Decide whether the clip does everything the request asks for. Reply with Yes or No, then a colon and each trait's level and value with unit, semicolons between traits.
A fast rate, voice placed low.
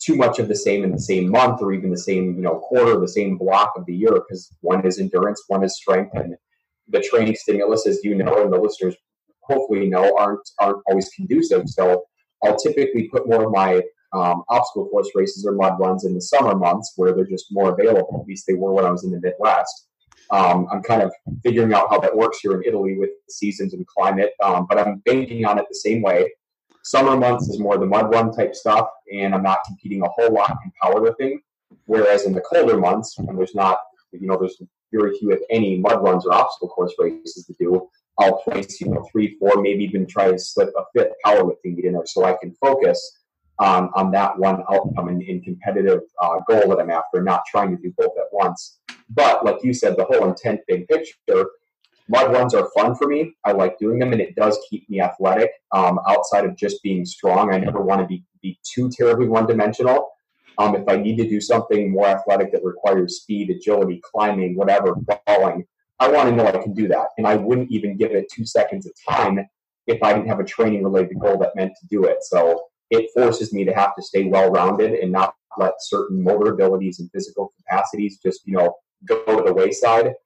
Yes: fast, 225 wpm; low, 105 Hz